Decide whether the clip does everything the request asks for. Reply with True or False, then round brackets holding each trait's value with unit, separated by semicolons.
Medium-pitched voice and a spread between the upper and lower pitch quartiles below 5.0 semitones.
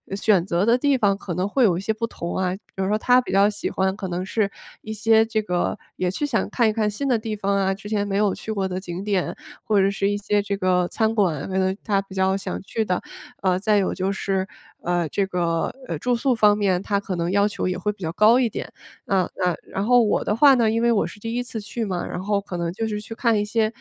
False (200 Hz; 2.6 semitones)